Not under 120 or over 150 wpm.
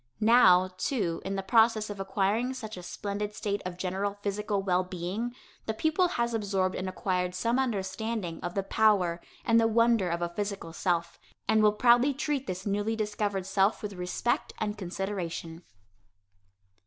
No: average, 165 wpm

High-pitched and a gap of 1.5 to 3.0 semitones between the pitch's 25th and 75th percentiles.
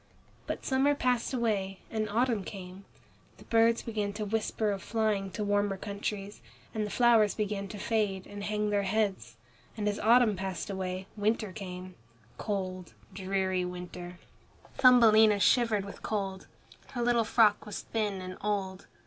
Yes: high, 205 Hz; narrow, 2.4 semitones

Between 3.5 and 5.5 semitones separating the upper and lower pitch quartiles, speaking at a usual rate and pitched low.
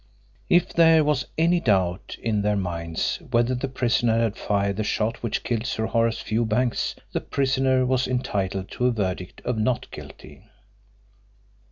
Yes: average, 4.0 semitones; average, 155 wpm; low, 115 Hz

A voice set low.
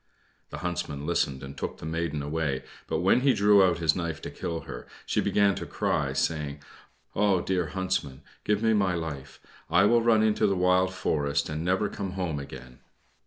Yes: very low, 85 Hz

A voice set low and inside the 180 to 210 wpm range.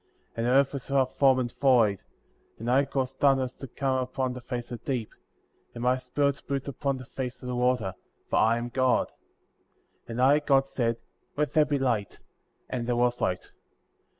Yes: low, 130 Hz; fast, 205 wpm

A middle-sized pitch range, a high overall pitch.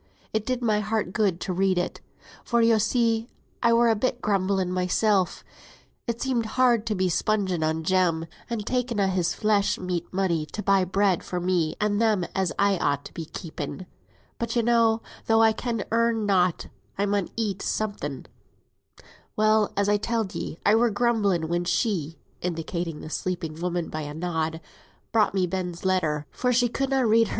Yes: average, 4.1 semitones; high, 200 Hz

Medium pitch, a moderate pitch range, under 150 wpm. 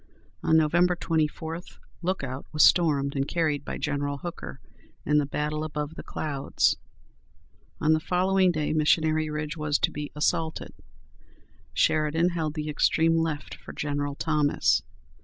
No: medium, 155 Hz; narrow, 1.8 semitones; average, 140 wpm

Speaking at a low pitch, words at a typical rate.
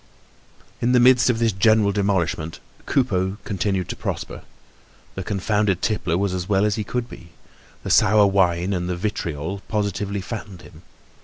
Yes: low, 100 Hz; average, 160 wpm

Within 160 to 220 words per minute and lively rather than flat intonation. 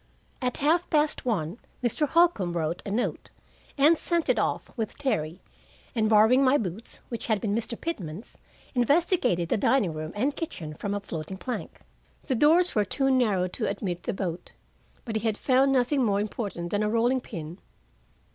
Yes: average, 175 wpm; wide, 6.3 semitones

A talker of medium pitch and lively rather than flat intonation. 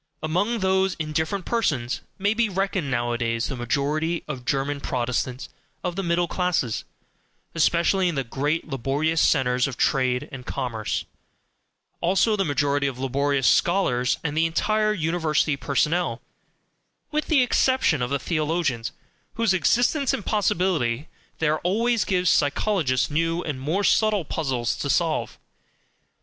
Yes: medium, 155 Hz; wide, 5.9 semitones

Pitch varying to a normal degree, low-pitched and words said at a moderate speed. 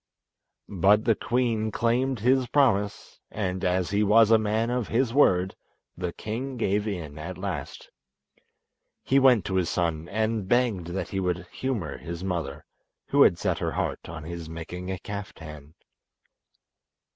Yes: average, 4.6 semitones; low, 100 Hz; average, 155 wpm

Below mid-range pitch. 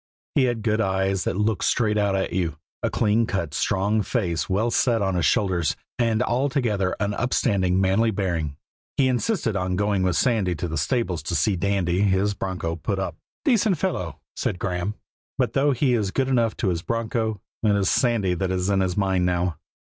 Yes: low, 100 Hz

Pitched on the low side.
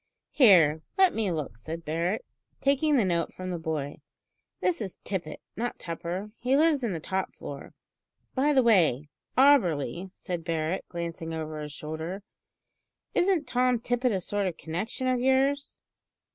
No: medium, 185 Hz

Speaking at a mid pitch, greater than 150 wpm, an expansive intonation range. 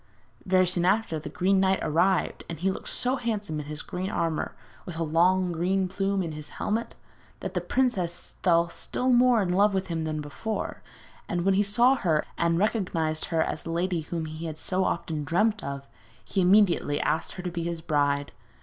No: medium, 180 Hz; average, 200 wpm; average, 3.3 semitones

